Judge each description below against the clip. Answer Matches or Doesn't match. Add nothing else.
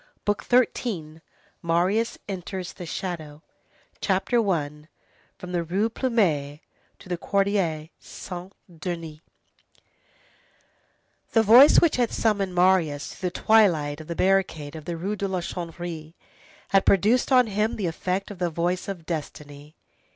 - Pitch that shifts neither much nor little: Matches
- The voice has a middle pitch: Matches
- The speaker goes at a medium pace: Doesn't match